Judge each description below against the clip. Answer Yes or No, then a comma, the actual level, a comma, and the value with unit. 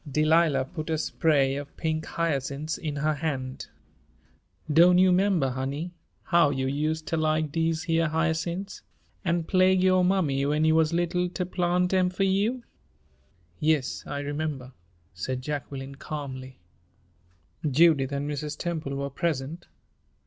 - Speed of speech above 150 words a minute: No, slow, 135 wpm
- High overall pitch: No, medium, 155 Hz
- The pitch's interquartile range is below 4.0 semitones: Yes, average, 3.5 semitones